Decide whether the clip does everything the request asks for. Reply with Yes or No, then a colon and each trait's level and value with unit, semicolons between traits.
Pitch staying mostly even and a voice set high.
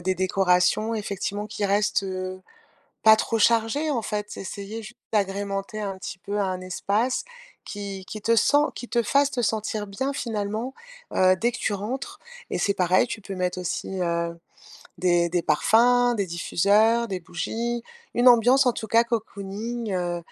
No: average, 3.6 semitones; high, 210 Hz